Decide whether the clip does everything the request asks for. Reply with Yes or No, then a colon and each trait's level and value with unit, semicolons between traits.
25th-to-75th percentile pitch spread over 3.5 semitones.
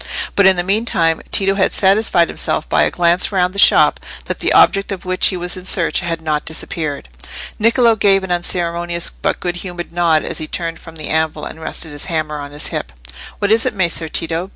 No: average, 2.9 semitones